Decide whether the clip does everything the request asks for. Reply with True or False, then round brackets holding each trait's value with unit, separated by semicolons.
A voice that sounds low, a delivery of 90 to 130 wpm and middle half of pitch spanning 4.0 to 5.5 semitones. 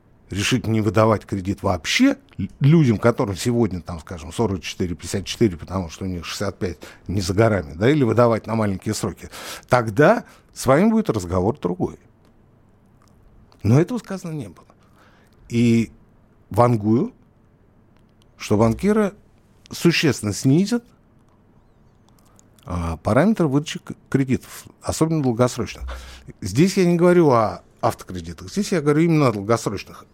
True (110 Hz; 115 wpm; 4.3 semitones)